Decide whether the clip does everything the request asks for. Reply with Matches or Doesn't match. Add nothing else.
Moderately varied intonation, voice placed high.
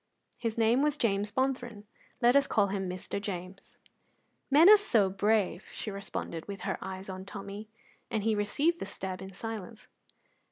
Matches